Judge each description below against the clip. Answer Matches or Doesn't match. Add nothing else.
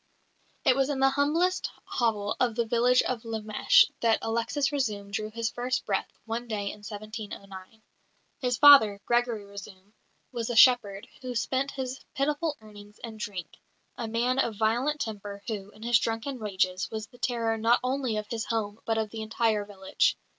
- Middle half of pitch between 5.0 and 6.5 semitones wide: Doesn't match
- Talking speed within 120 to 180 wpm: Matches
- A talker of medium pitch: Doesn't match